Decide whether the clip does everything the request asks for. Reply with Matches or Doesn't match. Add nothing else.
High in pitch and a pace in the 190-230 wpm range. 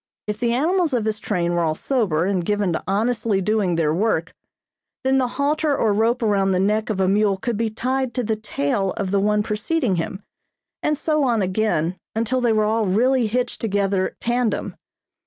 Matches